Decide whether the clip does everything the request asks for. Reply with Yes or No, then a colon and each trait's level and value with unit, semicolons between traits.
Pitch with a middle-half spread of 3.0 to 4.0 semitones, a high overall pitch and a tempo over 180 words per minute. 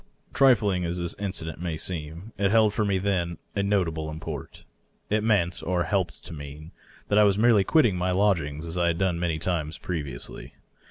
No: average, 3.6 semitones; very low, 90 Hz; average, 195 wpm